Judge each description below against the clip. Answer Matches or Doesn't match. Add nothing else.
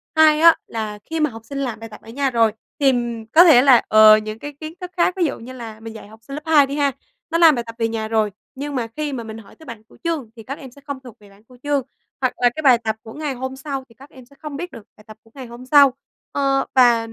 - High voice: Matches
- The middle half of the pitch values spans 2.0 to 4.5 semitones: Matches